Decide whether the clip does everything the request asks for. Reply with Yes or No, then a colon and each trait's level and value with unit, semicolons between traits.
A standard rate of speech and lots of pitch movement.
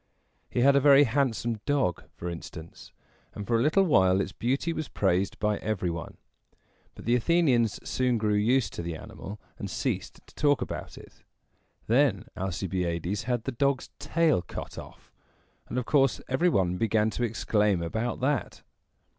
Yes: average, 165 wpm; wide, 5.9 semitones